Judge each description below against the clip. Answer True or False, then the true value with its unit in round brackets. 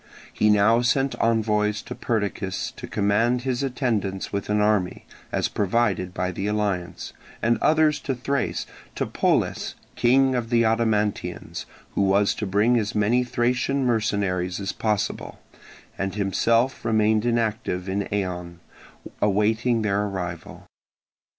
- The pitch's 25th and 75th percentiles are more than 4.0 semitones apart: False (3.1 semitones)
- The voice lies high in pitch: False (105 Hz)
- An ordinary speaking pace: False (130 wpm)